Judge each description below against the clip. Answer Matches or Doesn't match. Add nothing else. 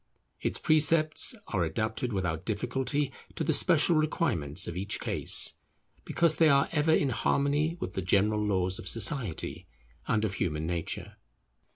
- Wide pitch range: Matches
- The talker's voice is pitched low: Matches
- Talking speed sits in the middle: Matches